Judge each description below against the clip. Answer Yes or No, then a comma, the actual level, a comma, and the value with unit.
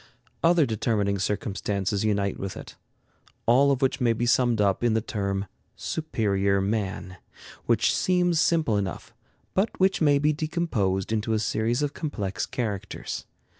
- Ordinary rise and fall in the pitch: No, wide, 6.3 semitones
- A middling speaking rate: Yes, average, 145 wpm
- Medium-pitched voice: No, low, 110 Hz